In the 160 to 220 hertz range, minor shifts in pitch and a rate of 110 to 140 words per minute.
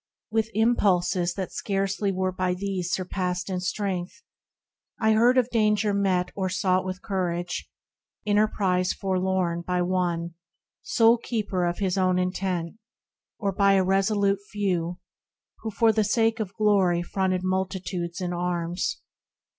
Yes: high, 190 Hz; narrow, 2.3 semitones; slow, 135 wpm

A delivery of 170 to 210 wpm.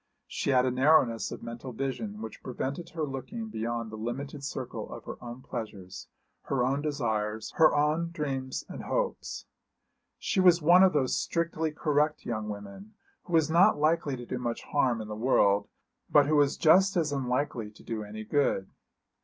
Yes: average, 180 wpm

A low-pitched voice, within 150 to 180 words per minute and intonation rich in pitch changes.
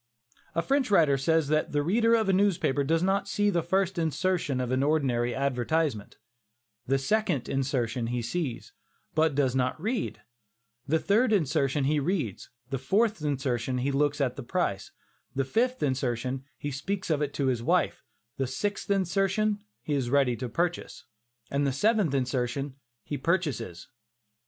No: medium, 145 Hz; average, 165 wpm; wide, 6.1 semitones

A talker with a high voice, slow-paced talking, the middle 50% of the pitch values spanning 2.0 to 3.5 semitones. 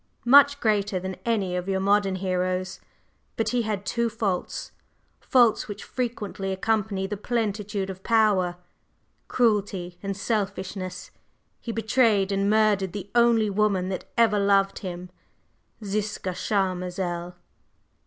Yes: high, 200 Hz; slow, 125 wpm; narrow, 2.6 semitones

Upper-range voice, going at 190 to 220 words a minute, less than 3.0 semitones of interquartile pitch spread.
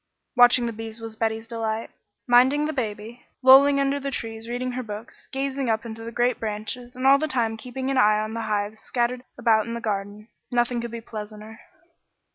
Yes: high, 235 Hz; average, 200 wpm; narrow, 2.4 semitones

